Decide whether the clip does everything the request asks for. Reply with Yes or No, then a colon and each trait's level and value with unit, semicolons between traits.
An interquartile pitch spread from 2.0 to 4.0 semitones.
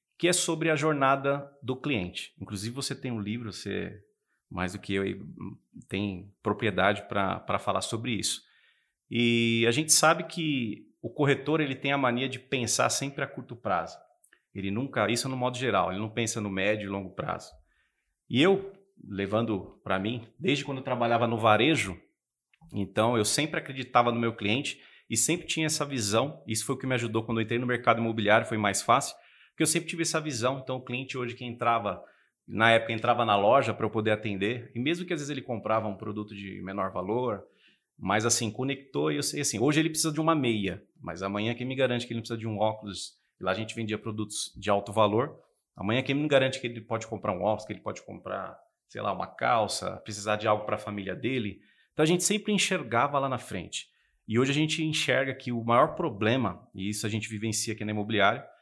No: average, 4.4 semitones